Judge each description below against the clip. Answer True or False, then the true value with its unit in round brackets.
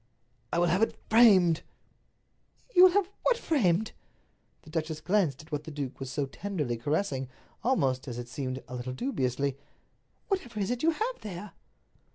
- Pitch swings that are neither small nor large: False (8.7 semitones)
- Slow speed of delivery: False (170 wpm)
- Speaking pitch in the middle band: True (170 Hz)